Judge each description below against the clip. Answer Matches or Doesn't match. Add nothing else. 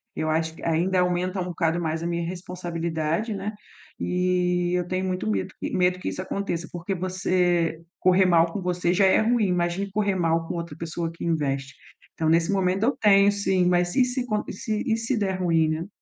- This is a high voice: Doesn't match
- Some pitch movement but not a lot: Doesn't match